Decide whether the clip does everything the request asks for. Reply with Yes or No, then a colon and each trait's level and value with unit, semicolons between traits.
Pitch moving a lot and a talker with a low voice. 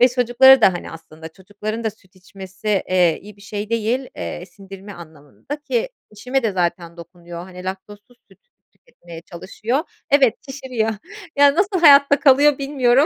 No: wide, 6.4 semitones; high, 210 Hz